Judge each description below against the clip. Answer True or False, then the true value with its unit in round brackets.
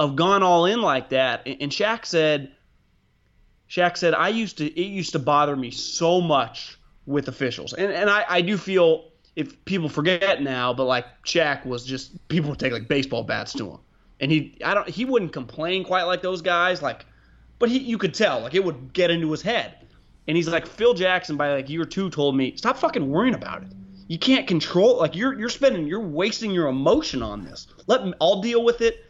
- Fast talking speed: True (215 wpm)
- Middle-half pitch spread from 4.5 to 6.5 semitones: True (5.6 semitones)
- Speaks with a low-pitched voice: False (170 Hz)